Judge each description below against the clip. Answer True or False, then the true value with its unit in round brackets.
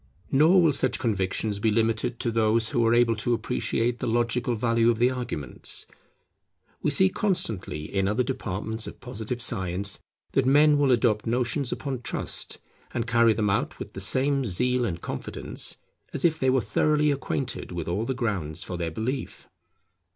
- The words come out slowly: False (175 wpm)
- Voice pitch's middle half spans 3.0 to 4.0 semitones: True (3.4 semitones)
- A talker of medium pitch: False (115 Hz)